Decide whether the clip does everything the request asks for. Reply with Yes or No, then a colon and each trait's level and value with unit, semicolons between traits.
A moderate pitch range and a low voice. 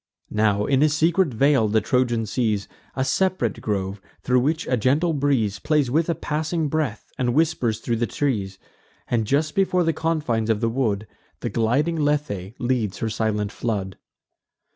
No: wide, 5.7 semitones; low, 125 Hz